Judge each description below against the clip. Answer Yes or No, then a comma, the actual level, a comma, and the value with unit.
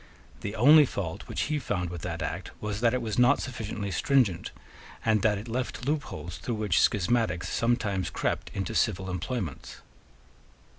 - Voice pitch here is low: Yes, low, 105 Hz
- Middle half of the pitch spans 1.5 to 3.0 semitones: No, average, 5.2 semitones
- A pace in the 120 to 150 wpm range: No, average, 160 wpm